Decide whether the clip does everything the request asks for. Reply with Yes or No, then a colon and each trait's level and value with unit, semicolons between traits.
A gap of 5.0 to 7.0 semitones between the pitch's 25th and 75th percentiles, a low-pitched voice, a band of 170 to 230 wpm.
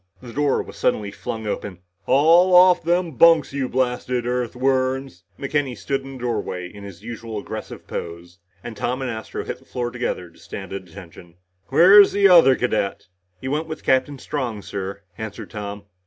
Yes: wide, 5.4 semitones; low, 125 Hz; average, 175 wpm